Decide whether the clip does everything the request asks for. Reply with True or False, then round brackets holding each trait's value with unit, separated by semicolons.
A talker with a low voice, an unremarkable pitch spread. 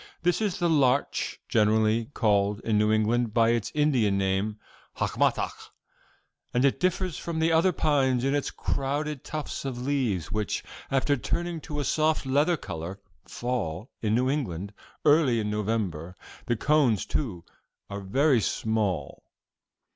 False (125 Hz; 5.7 semitones)